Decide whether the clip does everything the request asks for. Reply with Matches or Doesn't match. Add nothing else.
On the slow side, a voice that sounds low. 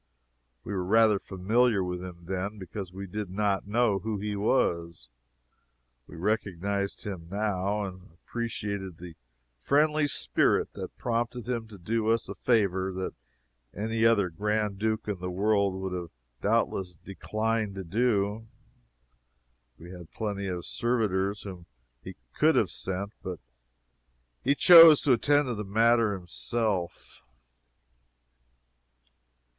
Matches